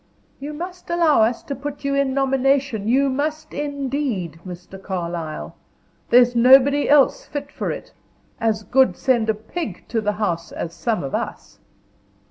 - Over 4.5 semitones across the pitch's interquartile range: Yes, average, 5.3 semitones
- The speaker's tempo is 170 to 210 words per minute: No, average, 155 wpm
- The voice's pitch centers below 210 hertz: No, very high, 260 Hz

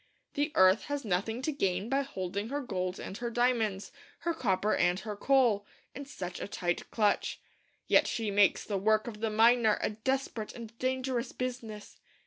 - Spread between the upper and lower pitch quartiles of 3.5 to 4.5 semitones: Yes, average, 4.1 semitones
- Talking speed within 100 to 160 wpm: No, average, 175 wpm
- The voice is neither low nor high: No, high, 220 Hz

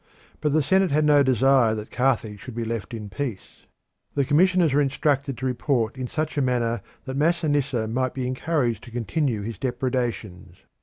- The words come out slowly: No, average, 175 wpm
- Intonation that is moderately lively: Yes, average, 3.8 semitones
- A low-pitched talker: Yes, low, 130 Hz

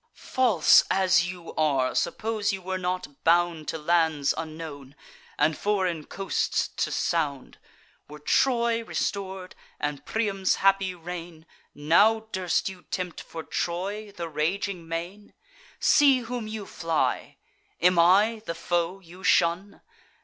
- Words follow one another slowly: Yes, slow, 125 wpm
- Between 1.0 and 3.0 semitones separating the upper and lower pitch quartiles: No, average, 3.5 semitones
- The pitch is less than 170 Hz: No, medium, 180 Hz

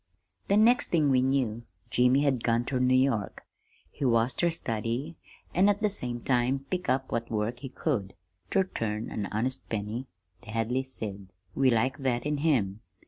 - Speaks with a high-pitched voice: No, low, 125 Hz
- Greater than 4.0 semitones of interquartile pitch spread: No, average, 3.4 semitones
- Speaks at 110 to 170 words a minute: No, average, 180 wpm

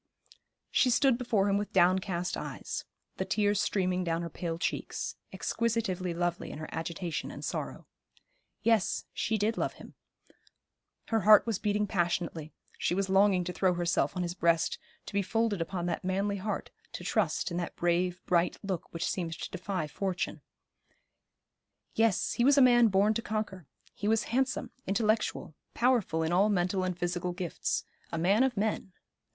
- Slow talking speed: No, average, 170 wpm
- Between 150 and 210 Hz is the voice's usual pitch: Yes, high, 190 Hz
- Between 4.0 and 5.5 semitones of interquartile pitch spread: No, average, 3.4 semitones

